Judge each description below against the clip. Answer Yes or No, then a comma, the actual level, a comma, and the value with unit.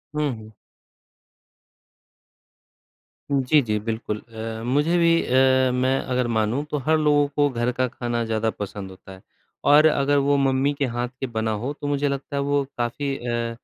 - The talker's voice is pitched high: No, low, 130 Hz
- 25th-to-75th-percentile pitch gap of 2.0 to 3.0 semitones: No, average, 3.6 semitones